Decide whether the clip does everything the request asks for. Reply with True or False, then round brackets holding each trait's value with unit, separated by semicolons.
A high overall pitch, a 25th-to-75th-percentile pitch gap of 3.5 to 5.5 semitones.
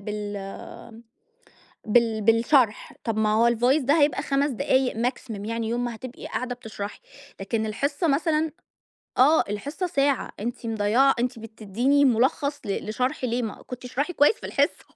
True (240 Hz; 4.1 semitones)